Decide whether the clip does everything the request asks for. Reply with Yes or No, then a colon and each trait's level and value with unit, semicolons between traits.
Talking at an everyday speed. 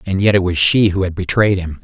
No: fast, 295 wpm